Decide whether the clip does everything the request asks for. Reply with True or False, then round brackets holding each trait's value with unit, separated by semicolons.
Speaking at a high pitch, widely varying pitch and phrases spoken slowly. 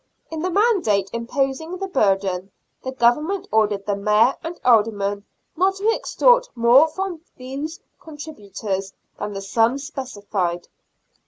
True (250 Hz; 7.9 semitones; 130 wpm)